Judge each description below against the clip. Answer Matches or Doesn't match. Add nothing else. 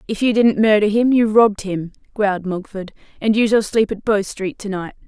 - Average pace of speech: Doesn't match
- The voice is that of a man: Doesn't match